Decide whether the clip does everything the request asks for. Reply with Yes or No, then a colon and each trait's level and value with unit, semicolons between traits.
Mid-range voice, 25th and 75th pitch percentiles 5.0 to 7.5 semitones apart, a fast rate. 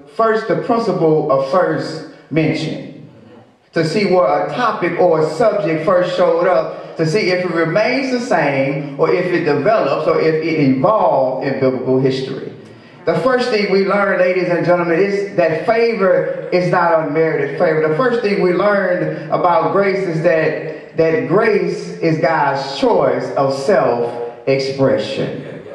No: medium, 175 Hz; wide, 5.4 semitones; average, 155 wpm